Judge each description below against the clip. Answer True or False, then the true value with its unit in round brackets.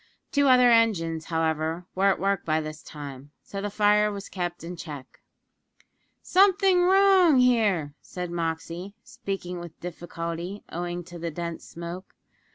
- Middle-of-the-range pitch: True (175 Hz)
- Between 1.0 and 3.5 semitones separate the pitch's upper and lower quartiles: False (4.2 semitones)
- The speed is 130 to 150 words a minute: True (145 wpm)